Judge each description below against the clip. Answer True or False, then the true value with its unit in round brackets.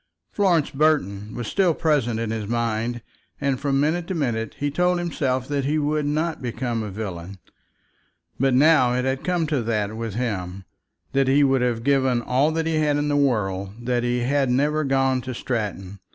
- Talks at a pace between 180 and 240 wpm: True (190 wpm)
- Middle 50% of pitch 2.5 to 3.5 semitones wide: False (4.3 semitones)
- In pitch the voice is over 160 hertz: False (130 Hz)